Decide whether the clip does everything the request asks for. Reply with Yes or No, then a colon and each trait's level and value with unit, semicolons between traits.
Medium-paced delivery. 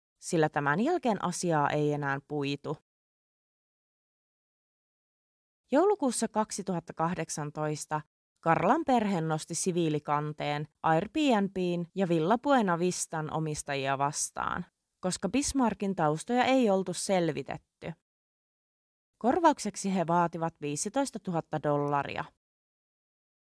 No: slow, 80 wpm